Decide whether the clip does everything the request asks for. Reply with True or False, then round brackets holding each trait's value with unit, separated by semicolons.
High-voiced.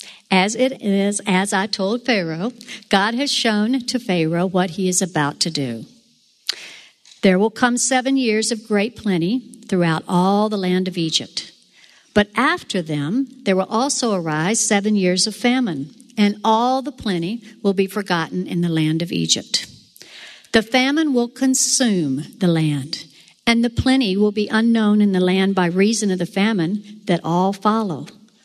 True (205 Hz)